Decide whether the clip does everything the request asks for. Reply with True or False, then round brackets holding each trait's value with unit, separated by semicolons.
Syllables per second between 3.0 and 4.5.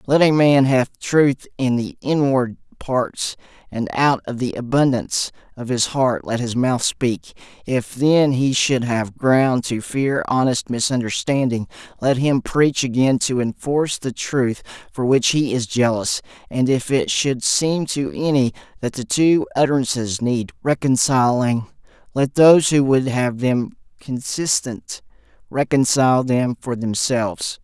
True (4.1 syllables/s)